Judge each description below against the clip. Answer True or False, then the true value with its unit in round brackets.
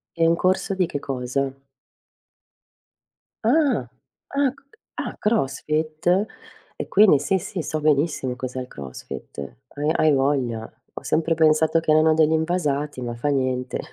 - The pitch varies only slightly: False (4.1 semitones)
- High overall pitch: False (155 Hz)